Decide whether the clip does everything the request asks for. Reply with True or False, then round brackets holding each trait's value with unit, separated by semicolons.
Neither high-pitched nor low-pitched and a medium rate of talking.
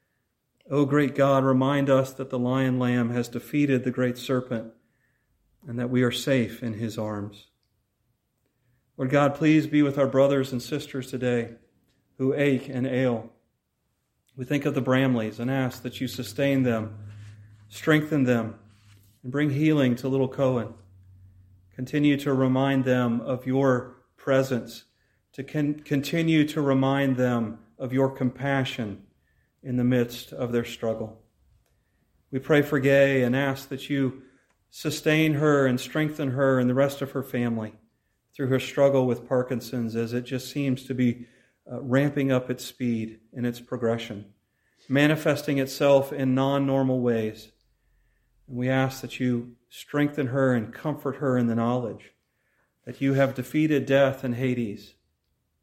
False (130 Hz; 150 wpm)